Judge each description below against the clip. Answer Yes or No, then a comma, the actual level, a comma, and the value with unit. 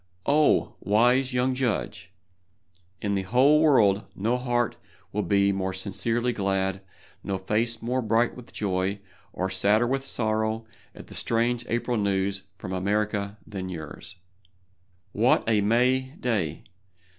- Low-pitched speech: Yes, low, 110 Hz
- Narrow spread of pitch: No, average, 3.8 semitones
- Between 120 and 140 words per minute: Yes, slow, 135 wpm